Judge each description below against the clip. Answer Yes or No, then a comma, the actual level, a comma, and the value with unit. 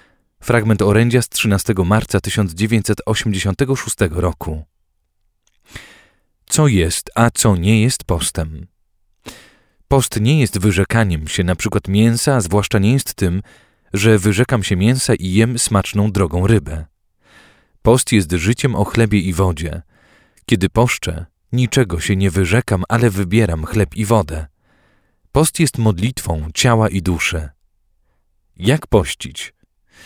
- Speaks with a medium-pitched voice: No, low, 105 Hz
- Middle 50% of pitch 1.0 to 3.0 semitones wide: No, average, 4.2 semitones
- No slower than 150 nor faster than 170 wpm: No, average, 125 wpm